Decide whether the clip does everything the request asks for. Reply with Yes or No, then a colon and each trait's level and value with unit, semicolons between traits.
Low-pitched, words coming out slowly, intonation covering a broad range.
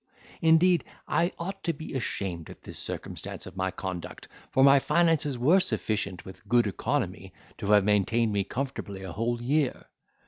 No: low, 120 Hz; average, 165 wpm; wide, 7.6 semitones